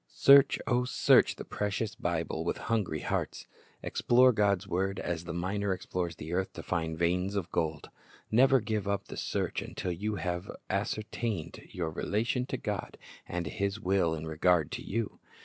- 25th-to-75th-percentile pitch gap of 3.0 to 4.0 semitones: Yes, average, 3.7 semitones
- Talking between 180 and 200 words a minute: No, average, 165 wpm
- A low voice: Yes, very low, 95 Hz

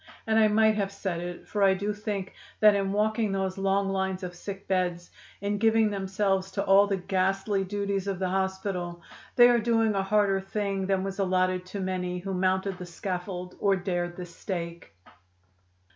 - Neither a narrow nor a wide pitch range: No, narrow, 1.7 semitones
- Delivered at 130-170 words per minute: No, average, 185 wpm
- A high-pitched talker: Yes, high, 195 Hz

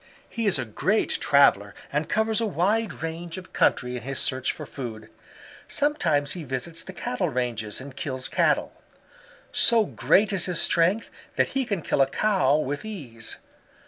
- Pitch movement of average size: No, wide, 7.6 semitones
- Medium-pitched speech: Yes, medium, 155 Hz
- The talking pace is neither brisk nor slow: Yes, average, 170 wpm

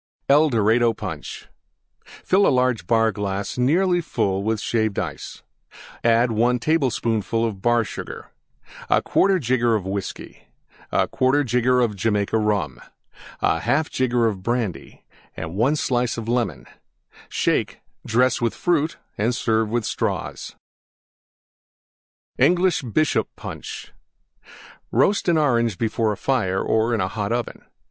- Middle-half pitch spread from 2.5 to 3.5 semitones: Yes, average, 3.2 semitones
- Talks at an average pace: No, slow, 110 wpm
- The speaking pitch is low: Yes, low, 115 Hz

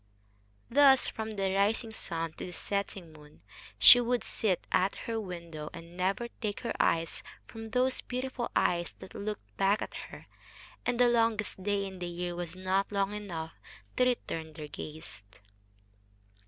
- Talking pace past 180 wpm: No, average, 160 wpm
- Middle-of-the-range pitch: No, high, 195 Hz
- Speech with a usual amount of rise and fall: Yes, average, 4.7 semitones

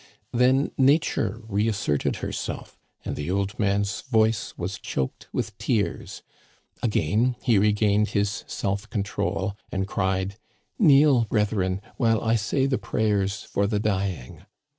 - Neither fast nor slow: No, slow, 130 wpm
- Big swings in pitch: No, narrow, 2.6 semitones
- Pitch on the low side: Yes, low, 105 Hz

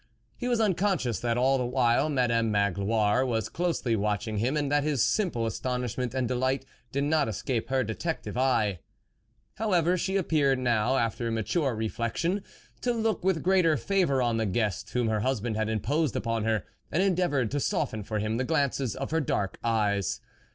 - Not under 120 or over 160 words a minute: No, average, 180 wpm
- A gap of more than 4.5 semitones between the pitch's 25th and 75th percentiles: Yes, wide, 5.5 semitones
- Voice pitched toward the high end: No, low, 125 Hz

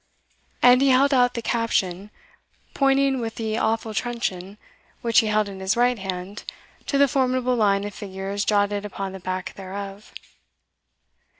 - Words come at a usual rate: Yes, average, 155 wpm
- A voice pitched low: No, high, 215 Hz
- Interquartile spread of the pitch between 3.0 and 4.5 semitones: Yes, average, 4.0 semitones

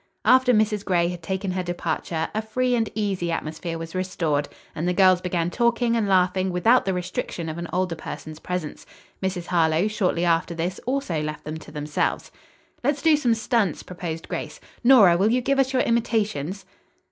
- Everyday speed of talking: Yes, average, 180 wpm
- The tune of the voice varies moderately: Yes, average, 4.8 semitones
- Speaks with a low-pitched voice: No, medium, 185 Hz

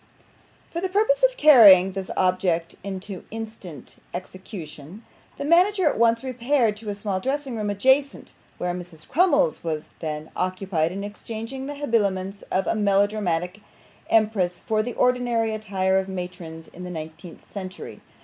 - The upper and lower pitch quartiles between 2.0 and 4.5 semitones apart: No, average, 4.9 semitones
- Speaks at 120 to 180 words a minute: Yes, average, 150 wpm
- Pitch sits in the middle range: No, high, 200 Hz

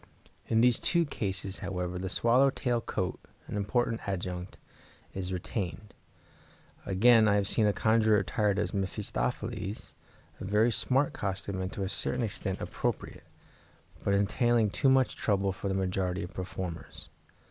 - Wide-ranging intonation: No, average, 3.3 semitones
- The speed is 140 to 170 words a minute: Yes, average, 145 wpm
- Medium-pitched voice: No, low, 100 Hz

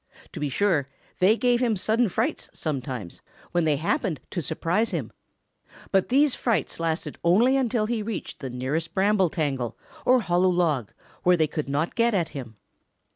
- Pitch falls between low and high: Yes, medium, 175 Hz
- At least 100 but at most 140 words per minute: No, average, 170 wpm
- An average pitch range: No, wide, 6.7 semitones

